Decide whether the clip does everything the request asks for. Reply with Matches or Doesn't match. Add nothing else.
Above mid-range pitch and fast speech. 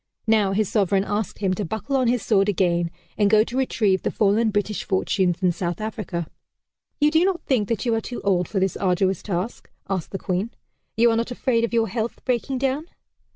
Matches